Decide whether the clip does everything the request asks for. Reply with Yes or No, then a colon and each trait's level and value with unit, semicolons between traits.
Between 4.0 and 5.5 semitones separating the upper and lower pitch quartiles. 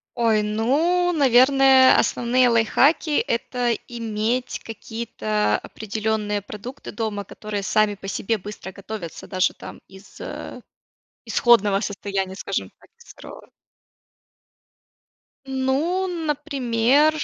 Yes: average, 4.3 semitones